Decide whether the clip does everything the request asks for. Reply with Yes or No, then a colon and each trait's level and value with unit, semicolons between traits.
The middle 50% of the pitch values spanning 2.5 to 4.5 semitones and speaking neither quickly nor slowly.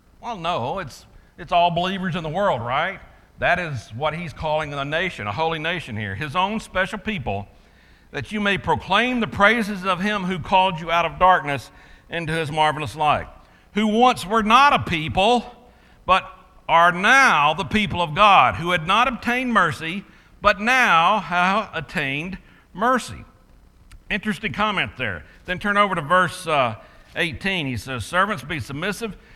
No: wide, 5.4 semitones; average, 165 wpm